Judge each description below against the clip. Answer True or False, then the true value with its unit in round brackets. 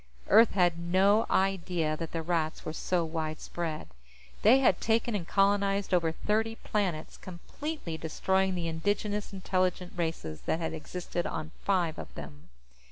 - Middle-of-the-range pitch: True (180 Hz)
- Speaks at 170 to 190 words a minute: False (145 wpm)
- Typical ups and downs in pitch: True (3.6 semitones)